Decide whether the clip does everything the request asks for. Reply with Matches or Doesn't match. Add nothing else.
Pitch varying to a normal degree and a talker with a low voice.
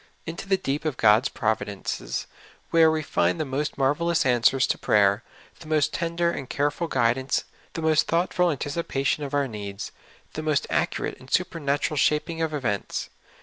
Doesn't match